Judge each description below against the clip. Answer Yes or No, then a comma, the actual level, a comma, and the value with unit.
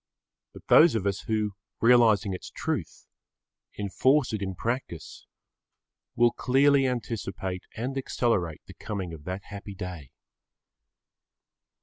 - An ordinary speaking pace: No, slow, 115 wpm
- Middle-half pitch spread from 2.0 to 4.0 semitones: No, average, 4.8 semitones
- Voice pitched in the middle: No, low, 105 Hz